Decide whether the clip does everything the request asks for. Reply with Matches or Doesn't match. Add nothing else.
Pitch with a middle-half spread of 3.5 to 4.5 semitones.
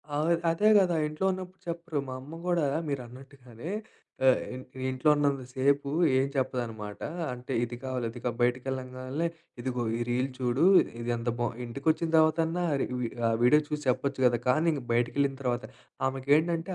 Matches